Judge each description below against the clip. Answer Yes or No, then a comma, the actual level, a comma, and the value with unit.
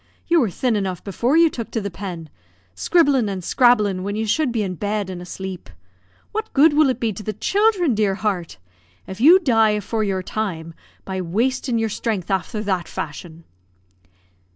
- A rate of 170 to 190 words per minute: Yes, average, 180 wpm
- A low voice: No, high, 215 Hz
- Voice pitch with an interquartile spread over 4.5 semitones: Yes, average, 5.0 semitones